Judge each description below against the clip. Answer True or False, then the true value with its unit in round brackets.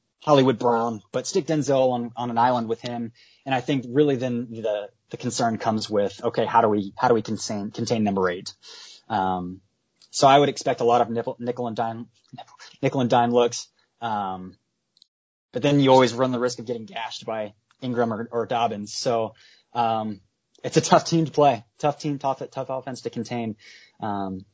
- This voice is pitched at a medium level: False (120 Hz)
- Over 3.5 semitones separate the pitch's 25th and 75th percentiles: False (3.1 semitones)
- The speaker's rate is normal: True (195 wpm)